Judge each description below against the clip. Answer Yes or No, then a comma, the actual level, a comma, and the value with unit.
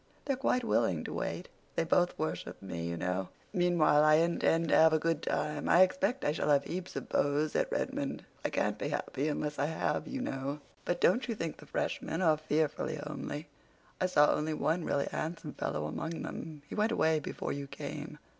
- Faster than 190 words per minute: Yes, average, 200 wpm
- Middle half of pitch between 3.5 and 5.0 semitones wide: No, average, 2.9 semitones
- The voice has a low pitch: No, medium, 155 Hz